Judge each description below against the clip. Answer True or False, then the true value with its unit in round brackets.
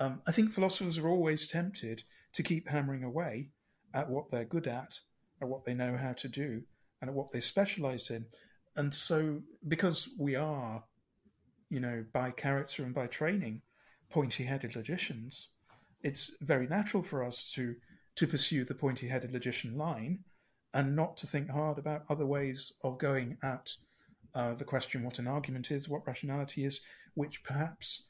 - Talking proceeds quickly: False (170 wpm)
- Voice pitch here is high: False (140 Hz)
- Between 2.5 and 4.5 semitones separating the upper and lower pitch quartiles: True (3.5 semitones)